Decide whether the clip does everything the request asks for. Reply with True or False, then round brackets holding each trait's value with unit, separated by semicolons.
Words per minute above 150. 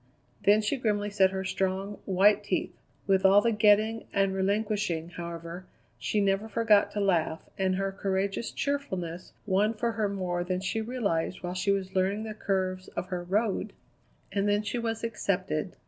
True (170 wpm)